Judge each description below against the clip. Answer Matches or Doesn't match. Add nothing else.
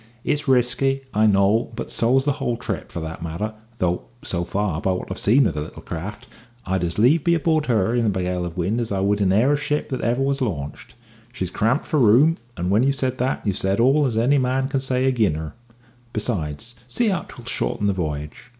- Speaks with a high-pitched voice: Doesn't match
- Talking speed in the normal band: Doesn't match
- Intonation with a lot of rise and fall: Matches